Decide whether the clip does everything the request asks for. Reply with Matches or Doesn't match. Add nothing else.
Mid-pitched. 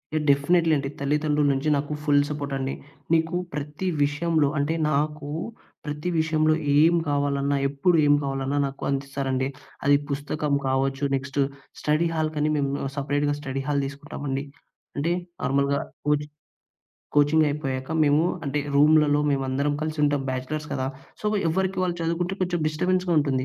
Matches